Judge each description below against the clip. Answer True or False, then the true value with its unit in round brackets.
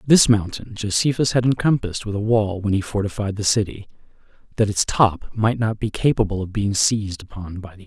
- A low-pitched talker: True (105 Hz)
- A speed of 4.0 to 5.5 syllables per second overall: False (6.0 syllables/s)